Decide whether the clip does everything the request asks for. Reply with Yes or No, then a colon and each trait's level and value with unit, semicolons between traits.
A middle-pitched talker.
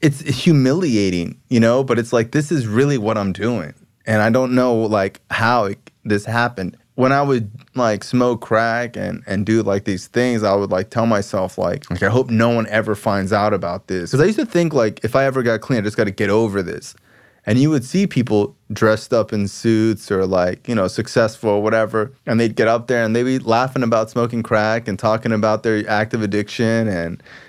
No: low, 115 Hz